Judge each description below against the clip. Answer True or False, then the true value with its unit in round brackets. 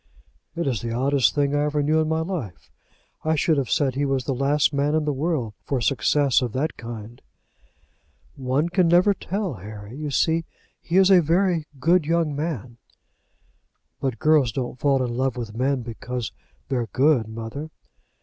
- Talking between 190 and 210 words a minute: False (180 wpm)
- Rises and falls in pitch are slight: False (4.2 semitones)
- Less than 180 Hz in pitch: True (140 Hz)